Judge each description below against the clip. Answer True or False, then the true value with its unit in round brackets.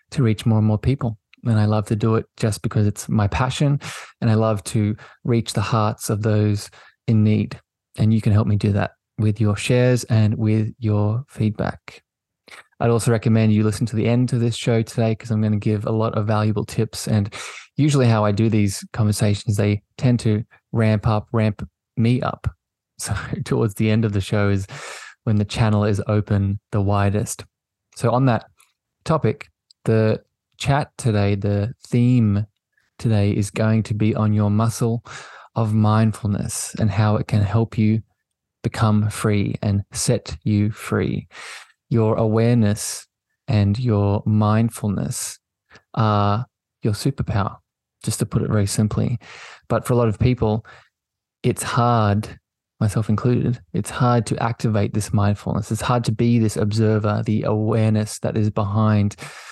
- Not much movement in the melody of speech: True (1.8 semitones)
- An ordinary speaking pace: True (165 wpm)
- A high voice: False (110 Hz)